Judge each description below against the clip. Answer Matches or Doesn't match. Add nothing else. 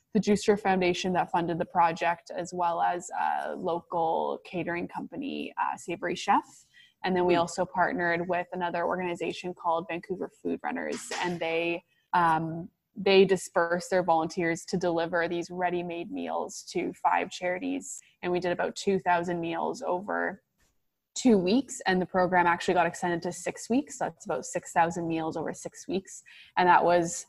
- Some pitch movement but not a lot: Doesn't match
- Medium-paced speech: Matches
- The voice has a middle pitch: Matches